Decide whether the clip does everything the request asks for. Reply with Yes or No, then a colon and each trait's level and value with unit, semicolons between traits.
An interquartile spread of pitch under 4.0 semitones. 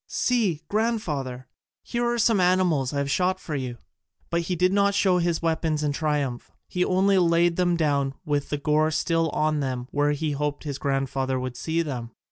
No: average, 4.3 semitones